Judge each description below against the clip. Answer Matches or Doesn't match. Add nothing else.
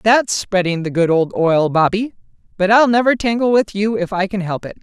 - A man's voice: Doesn't match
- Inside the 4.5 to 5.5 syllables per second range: Matches